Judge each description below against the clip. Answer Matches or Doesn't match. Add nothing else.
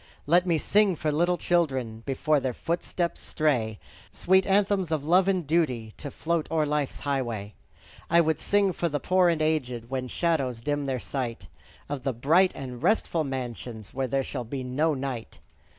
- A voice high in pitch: Doesn't match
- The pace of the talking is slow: Doesn't match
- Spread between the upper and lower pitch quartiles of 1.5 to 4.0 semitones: Doesn't match